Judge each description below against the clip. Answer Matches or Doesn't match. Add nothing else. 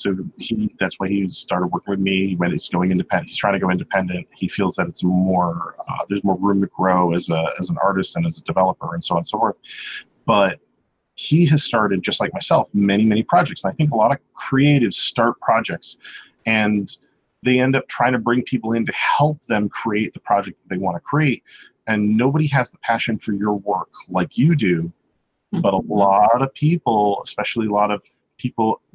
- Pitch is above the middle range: Doesn't match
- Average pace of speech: Doesn't match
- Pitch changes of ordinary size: Matches